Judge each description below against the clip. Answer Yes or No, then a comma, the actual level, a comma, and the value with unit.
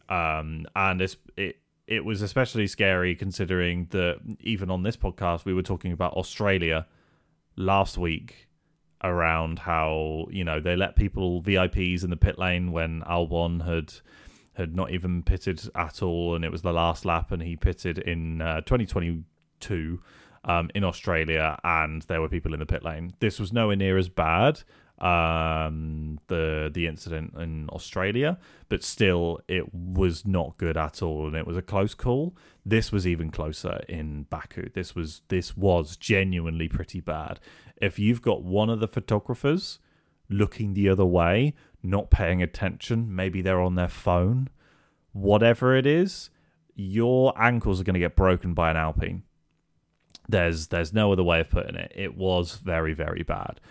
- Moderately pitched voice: No, very low, 90 Hz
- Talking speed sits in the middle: Yes, average, 165 wpm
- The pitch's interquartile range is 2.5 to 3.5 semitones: Yes, average, 3.1 semitones